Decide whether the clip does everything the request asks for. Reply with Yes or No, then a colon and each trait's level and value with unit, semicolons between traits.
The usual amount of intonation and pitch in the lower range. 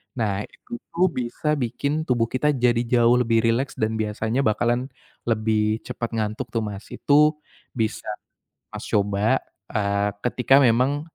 Yes: average, 3.0 semitones; low, 115 Hz